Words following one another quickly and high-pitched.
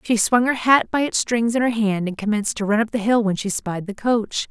Yes: fast, 295 wpm; high, 220 Hz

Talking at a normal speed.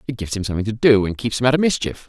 No: fast, 345 wpm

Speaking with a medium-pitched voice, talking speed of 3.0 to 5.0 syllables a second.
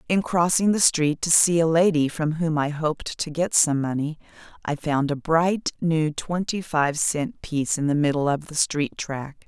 Yes: medium, 155 Hz; 4.5 syllables/s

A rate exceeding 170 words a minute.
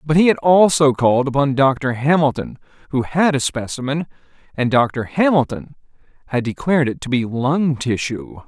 No: average, 155 wpm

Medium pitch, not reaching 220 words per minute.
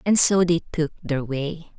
Yes: medium, 160 Hz; average, 200 wpm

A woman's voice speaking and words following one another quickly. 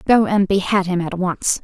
Yes: female; fast, 220 wpm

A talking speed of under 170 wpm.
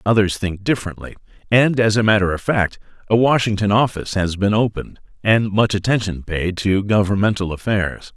Yes: average, 160 wpm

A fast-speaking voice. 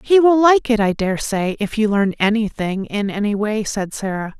Yes: fast, 220 wpm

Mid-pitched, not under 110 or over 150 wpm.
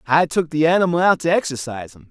No: medium, 160 Hz; fast, 230 wpm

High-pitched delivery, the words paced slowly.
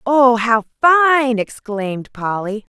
Yes: high, 240 Hz; slow, 105 wpm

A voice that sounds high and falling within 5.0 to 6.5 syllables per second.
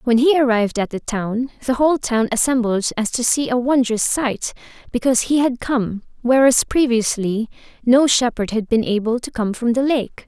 Yes: high, 240 Hz; 5.1 syllables/s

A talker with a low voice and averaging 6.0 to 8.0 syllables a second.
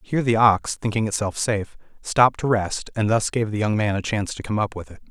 Yes: low, 105 Hz; 6.1 syllables/s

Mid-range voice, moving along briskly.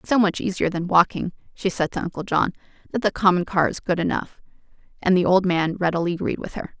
Yes: medium, 180 Hz; fast, 230 wpm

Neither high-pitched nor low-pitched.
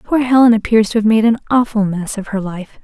No: high, 220 Hz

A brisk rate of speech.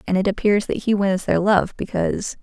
Yes: fast, 225 wpm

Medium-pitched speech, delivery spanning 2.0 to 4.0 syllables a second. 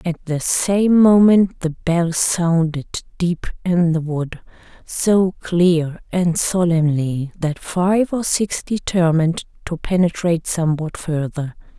Yes: medium, 170 Hz; 3.6 syllables/s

